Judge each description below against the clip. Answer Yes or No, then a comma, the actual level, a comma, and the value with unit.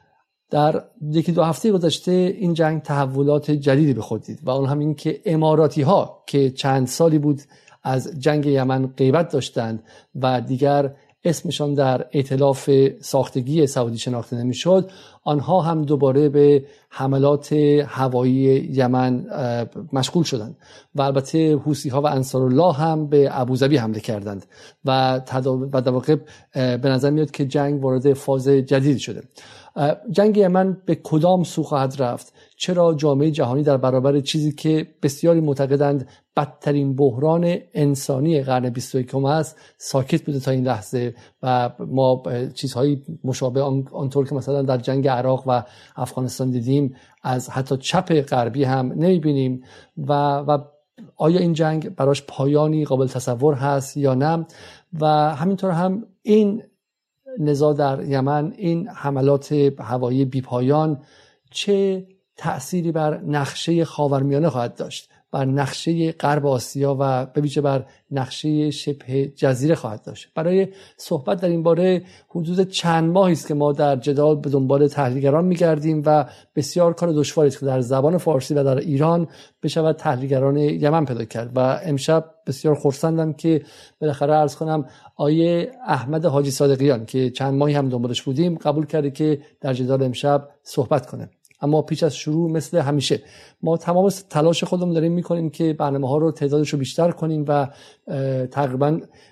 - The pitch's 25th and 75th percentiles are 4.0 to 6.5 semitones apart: No, average, 2.9 semitones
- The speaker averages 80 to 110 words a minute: No, average, 145 wpm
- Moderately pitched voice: Yes, medium, 145 Hz